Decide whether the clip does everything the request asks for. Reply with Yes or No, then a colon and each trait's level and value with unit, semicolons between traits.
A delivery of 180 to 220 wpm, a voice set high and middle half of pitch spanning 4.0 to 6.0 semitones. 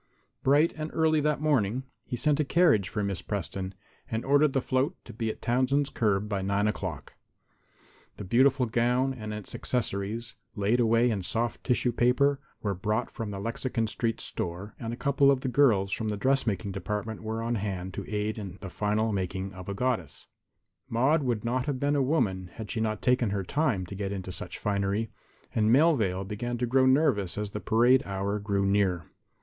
No: average, 190 wpm; low, 110 Hz; average, 4.5 semitones